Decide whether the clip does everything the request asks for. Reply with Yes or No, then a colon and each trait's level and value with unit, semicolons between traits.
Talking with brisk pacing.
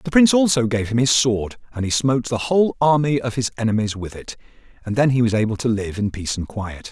Yes: fast, 250 wpm